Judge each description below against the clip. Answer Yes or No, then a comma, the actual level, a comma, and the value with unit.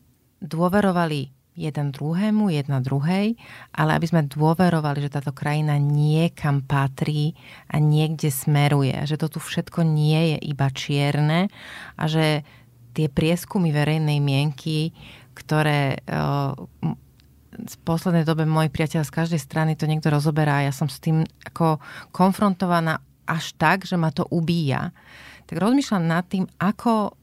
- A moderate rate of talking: Yes, average, 135 wpm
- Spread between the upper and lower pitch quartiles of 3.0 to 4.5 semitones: No, narrow, 2.5 semitones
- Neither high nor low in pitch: Yes, medium, 155 Hz